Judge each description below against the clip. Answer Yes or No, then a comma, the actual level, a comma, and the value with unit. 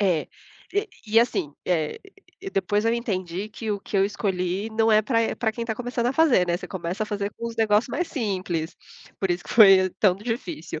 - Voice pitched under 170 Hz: No, high, 205 Hz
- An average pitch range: Yes, average, 3.7 semitones